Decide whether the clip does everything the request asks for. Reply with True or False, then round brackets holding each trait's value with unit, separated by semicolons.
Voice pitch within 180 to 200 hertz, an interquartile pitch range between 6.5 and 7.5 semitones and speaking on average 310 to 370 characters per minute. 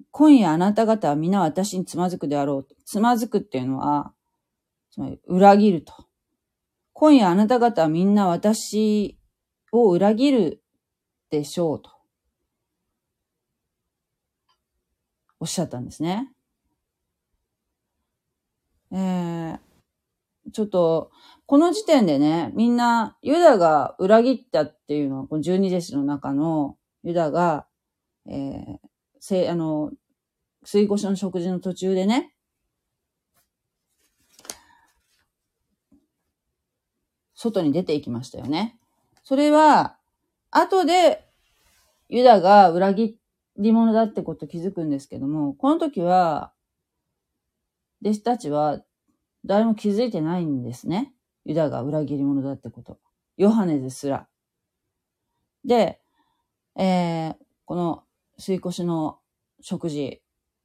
False (185 Hz; 6.9 semitones; 210 characters per minute)